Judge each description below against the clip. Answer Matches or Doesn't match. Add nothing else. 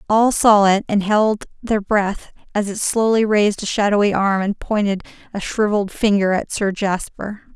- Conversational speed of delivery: Matches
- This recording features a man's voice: Doesn't match